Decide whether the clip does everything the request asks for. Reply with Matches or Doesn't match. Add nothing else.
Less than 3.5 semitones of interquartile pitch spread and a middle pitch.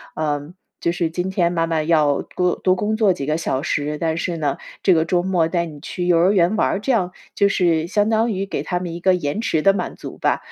Matches